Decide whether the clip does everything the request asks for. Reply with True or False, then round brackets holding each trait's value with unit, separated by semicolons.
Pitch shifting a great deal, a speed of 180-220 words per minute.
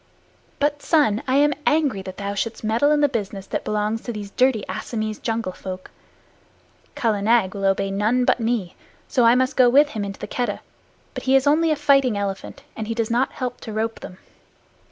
False (4.4 semitones; 205 wpm)